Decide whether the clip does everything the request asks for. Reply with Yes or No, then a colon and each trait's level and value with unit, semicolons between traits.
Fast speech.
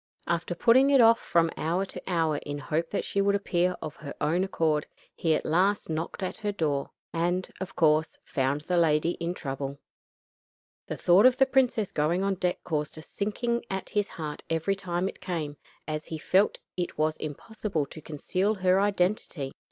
No: average, 190 wpm